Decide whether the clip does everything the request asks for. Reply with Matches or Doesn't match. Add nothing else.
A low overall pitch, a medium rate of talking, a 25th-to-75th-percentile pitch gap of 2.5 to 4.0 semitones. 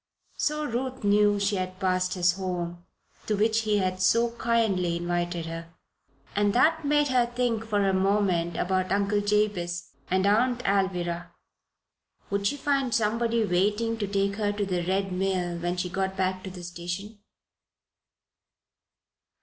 Doesn't match